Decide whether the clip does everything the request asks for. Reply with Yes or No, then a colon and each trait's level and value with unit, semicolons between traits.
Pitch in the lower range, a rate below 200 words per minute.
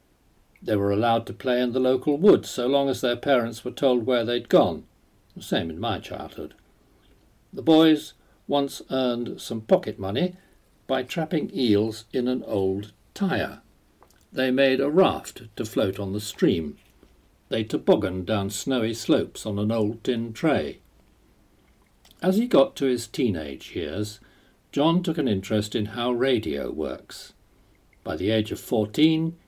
Yes: low, 125 Hz; average, 155 wpm